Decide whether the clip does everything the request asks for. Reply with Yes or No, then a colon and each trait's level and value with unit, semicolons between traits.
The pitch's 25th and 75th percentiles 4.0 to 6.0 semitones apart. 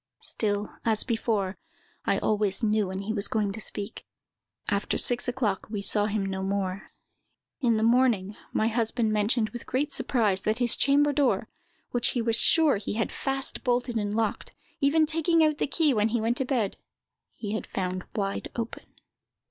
No: average, 3.5 semitones